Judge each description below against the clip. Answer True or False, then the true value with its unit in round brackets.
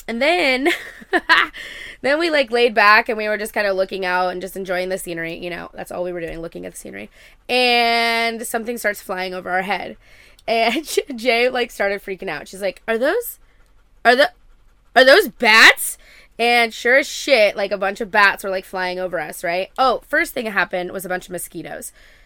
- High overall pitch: True (210 Hz)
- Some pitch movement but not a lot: True (4.8 semitones)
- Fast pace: True (210 wpm)